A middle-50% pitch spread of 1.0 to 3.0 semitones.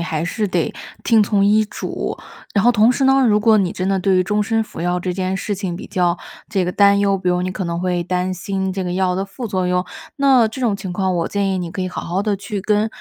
Yes: narrow, 2.6 semitones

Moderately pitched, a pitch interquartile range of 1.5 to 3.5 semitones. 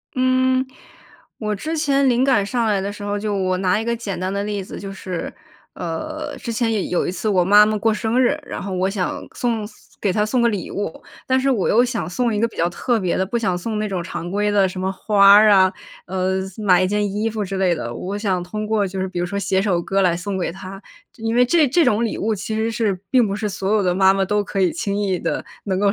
No: high, 205 Hz; average, 3.0 semitones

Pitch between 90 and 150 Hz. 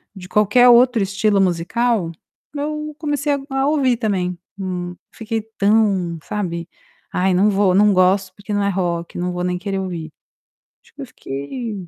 No: high, 200 Hz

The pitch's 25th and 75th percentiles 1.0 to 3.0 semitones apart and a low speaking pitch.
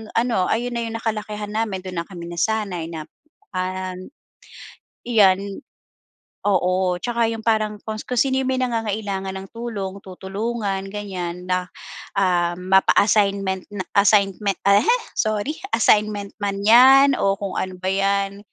No: average, 2.7 semitones; high, 200 Hz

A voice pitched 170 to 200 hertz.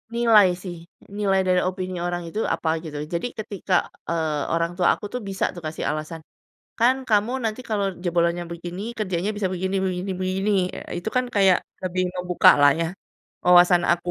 Yes: medium, 185 Hz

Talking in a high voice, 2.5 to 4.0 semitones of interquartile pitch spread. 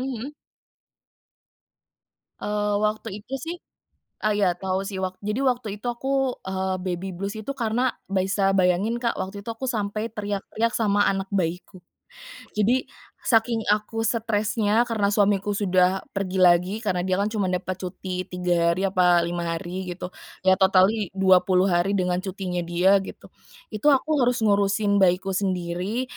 Yes: high, 195 Hz; average, 2.8 semitones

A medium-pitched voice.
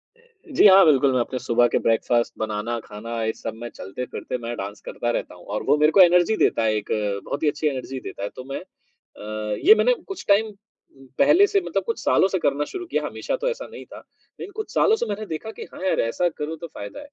Yes: medium, 150 Hz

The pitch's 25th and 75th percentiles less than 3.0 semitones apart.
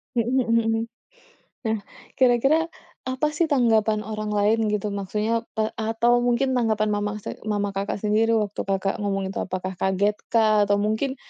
Yes: narrow, 2.6 semitones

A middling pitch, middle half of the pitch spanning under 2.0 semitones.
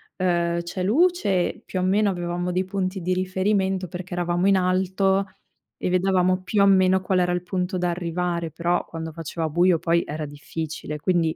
Yes: medium, 180 Hz; narrow, 1.6 semitones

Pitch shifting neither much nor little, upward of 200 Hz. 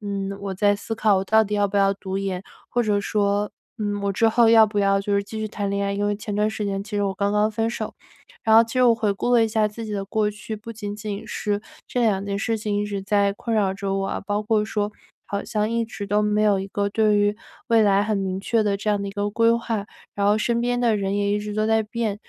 No: narrow, 1.5 semitones; high, 210 Hz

